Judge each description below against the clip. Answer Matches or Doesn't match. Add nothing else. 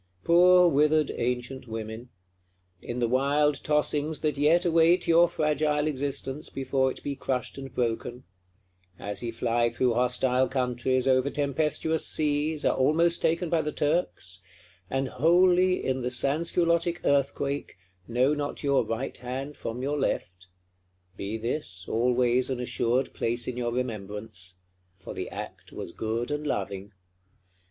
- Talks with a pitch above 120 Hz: Matches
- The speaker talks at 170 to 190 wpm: Doesn't match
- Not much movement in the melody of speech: Doesn't match